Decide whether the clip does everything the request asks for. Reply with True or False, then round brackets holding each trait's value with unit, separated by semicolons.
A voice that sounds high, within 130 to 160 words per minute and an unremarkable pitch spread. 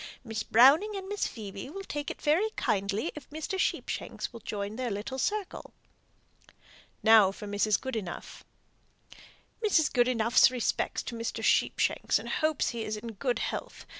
False (240 Hz; 150 wpm; 6.1 semitones)